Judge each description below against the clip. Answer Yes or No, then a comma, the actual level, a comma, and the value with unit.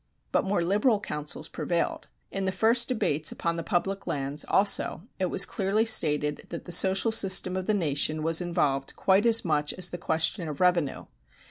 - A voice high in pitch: No, medium, 180 Hz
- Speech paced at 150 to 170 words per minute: No, average, 185 wpm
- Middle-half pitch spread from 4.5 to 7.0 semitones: No, average, 4.0 semitones